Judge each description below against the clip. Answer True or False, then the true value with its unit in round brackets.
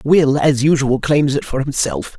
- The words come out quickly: False (195 wpm)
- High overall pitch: False (135 Hz)